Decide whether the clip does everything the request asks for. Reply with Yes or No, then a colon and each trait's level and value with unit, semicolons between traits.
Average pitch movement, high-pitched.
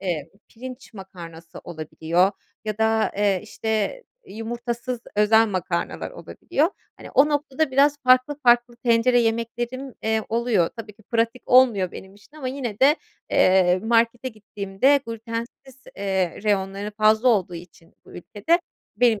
Yes: average, 4.3 semitones; high, 225 Hz